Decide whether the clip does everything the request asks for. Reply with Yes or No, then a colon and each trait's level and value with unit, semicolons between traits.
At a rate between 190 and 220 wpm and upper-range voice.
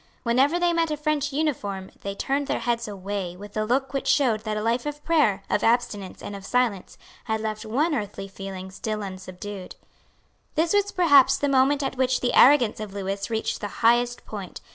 Yes: average, 195 wpm; high, 230 Hz